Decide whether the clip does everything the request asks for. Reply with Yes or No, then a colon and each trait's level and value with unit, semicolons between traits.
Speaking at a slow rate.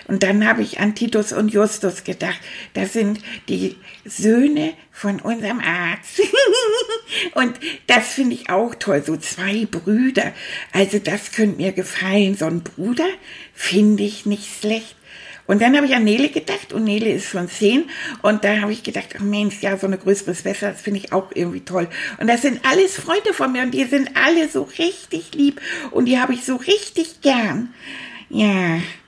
No: average, 185 wpm